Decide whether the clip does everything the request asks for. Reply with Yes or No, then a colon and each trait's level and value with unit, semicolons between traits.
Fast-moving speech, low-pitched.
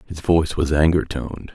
No: average, 195 wpm; very low, 80 Hz